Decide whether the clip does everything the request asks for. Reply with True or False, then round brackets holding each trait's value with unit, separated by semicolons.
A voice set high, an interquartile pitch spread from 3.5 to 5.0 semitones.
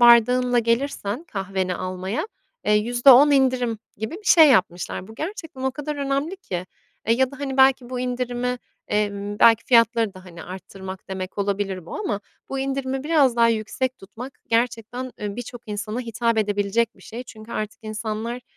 True (235 Hz; 4.0 semitones)